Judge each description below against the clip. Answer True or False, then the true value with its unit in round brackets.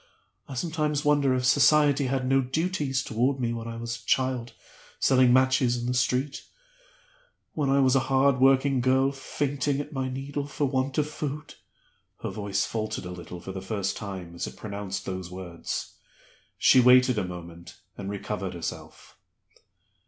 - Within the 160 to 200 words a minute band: True (165 wpm)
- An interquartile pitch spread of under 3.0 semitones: False (4.6 semitones)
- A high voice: False (130 Hz)